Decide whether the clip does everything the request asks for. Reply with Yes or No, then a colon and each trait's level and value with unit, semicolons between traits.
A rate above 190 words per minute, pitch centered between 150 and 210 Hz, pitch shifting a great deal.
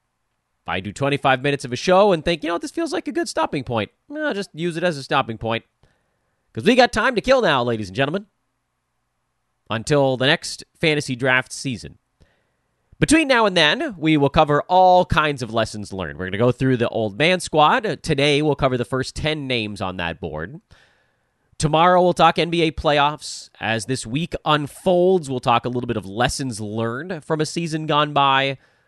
No: average, 200 wpm; medium, 140 Hz; wide, 6.2 semitones